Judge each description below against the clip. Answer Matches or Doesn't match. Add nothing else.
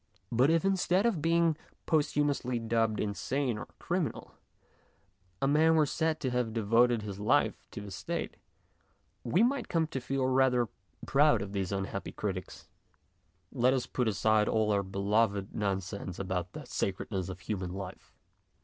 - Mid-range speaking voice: Doesn't match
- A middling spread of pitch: Doesn't match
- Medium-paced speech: Matches